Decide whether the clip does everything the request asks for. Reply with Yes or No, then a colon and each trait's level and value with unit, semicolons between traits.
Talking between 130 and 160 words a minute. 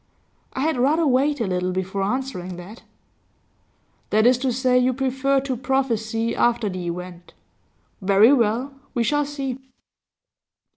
Yes: average, 140 wpm